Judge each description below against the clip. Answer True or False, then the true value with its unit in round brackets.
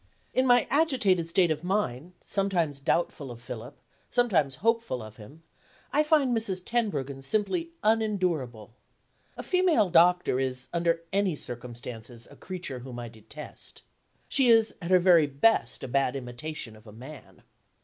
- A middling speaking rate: True (150 wpm)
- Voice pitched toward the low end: False (165 Hz)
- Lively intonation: True (8.8 semitones)